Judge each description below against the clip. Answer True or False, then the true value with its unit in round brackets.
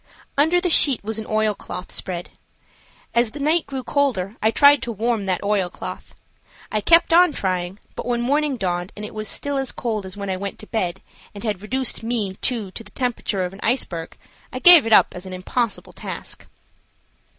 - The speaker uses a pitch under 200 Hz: False (220 Hz)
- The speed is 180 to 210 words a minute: True (195 wpm)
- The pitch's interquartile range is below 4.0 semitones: False (5.4 semitones)